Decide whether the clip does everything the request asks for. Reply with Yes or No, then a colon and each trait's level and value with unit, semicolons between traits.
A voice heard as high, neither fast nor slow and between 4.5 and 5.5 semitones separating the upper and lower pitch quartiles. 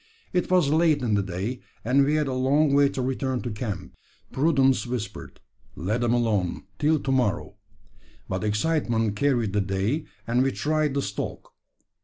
No: low, 125 Hz; average, 170 wpm; average, 5.1 semitones